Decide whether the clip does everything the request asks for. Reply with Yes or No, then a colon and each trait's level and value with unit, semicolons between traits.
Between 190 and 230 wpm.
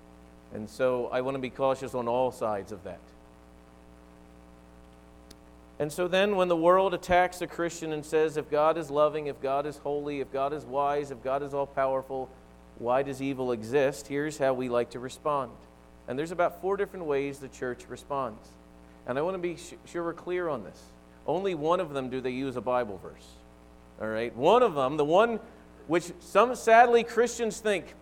Yes: average, 195 wpm